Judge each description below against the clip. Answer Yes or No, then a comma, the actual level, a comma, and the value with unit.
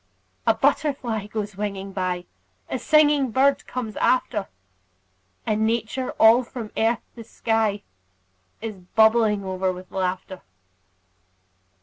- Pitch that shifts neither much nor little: Yes, average, 3.4 semitones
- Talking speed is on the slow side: Yes, slow, 110 wpm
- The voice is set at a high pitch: Yes, high, 220 Hz